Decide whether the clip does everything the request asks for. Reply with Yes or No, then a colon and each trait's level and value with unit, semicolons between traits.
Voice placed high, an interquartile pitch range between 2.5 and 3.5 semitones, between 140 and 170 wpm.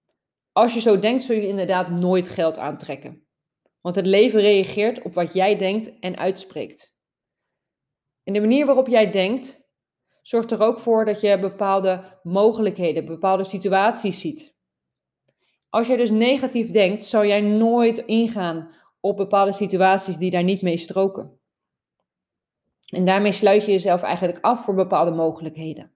Yes: high, 195 Hz; average, 3.2 semitones; average, 150 wpm